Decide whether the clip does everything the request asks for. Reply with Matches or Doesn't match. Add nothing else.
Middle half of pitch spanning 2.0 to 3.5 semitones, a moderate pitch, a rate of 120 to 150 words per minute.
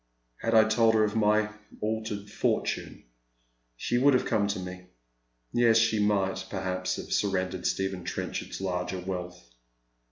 Doesn't match